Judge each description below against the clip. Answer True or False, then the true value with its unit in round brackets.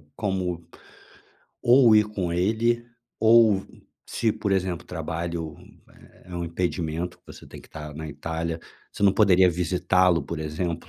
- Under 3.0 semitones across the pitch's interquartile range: False (3.4 semitones)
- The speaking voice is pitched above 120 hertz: False (90 Hz)